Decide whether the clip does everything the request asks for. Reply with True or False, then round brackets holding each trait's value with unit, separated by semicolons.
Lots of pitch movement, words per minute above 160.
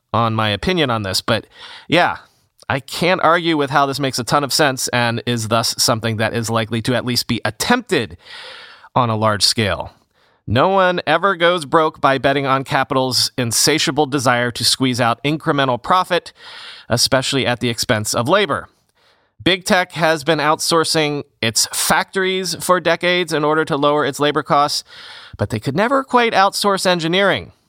True (5.9 semitones; 170 wpm)